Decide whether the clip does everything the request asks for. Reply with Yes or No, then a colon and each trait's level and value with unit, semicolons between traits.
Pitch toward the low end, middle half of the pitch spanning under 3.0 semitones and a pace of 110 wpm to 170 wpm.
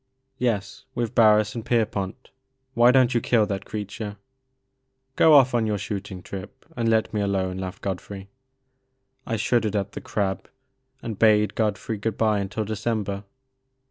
Yes: low, 105 Hz; narrow, 2.5 semitones; average, 150 wpm